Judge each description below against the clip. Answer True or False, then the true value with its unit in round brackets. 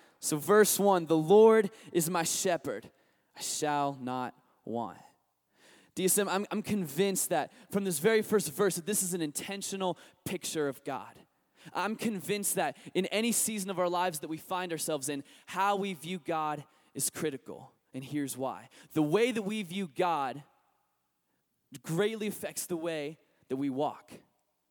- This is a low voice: False (180 Hz)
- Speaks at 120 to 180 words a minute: True (160 wpm)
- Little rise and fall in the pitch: False (4.8 semitones)